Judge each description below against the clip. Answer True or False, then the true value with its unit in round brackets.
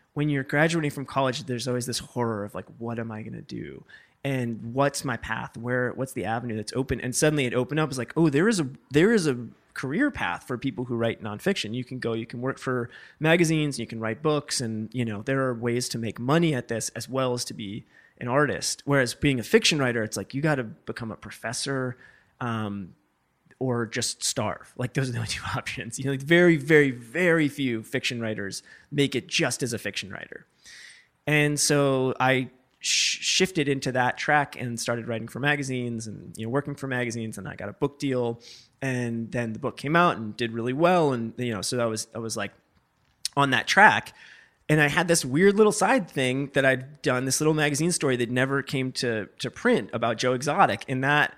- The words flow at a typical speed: False (225 wpm)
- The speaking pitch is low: True (130 Hz)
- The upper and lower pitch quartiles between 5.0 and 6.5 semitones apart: False (3.6 semitones)